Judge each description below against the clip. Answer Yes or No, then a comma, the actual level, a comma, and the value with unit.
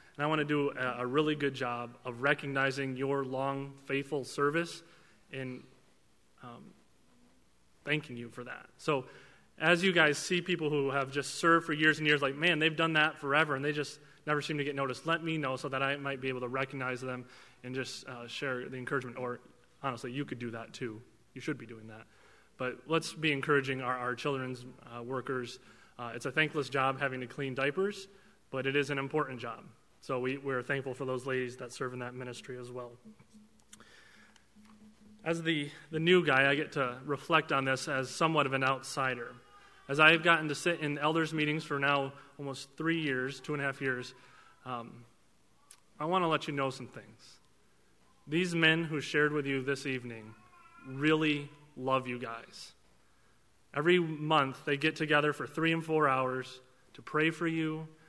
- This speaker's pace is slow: No, average, 190 wpm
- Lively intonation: No, average, 3.4 semitones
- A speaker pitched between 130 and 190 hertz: Yes, medium, 140 Hz